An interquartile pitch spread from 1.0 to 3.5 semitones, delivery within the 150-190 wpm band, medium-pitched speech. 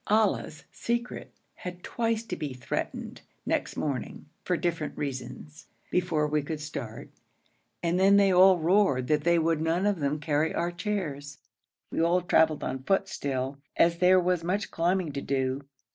No: average, 3.9 semitones; average, 160 wpm; medium, 165 Hz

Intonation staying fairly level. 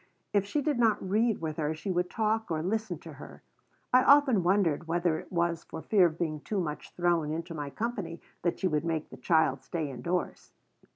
No: average, 4.7 semitones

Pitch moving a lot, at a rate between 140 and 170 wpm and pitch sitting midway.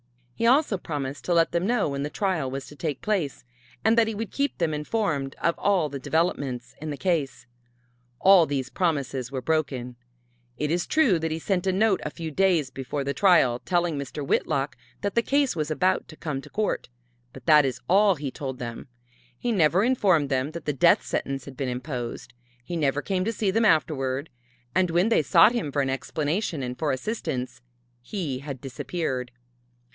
No: wide, 5.7 semitones; average, 200 wpm; medium, 155 Hz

